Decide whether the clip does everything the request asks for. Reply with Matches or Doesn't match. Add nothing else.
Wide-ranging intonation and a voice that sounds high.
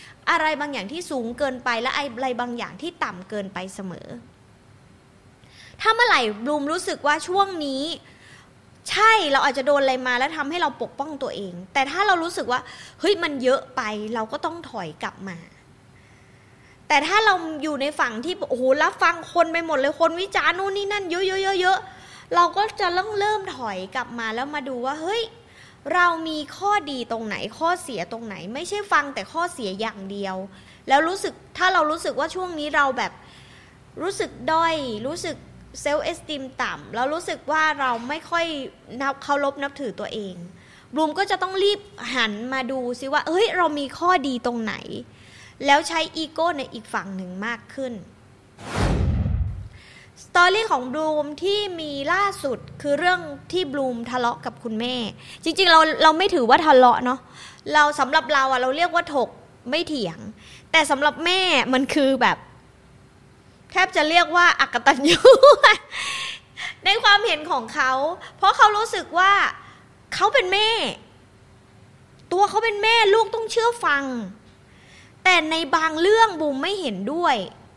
Matches